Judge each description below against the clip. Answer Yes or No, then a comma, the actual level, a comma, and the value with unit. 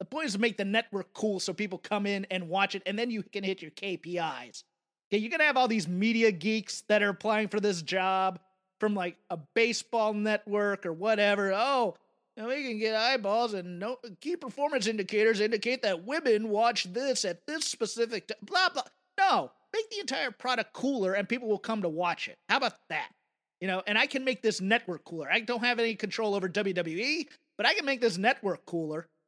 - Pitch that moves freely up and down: No, average, 4.1 semitones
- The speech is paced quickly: Yes, fast, 215 wpm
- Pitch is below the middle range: No, high, 215 Hz